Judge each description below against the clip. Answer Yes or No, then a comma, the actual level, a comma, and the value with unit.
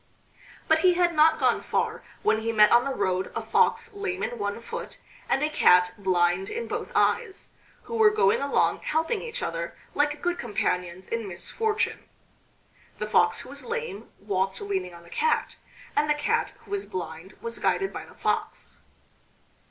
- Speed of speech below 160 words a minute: No, average, 175 wpm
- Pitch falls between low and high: No, high, 240 Hz